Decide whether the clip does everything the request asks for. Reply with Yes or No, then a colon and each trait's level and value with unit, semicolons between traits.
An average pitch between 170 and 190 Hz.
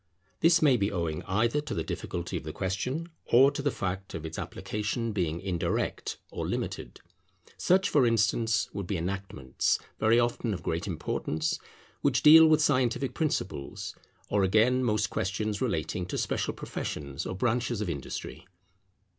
No: low, 105 Hz